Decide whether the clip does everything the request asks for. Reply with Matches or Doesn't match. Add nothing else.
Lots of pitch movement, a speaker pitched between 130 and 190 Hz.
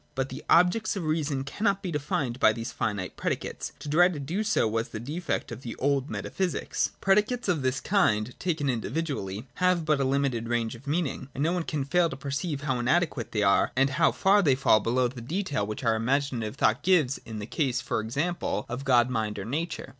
Matches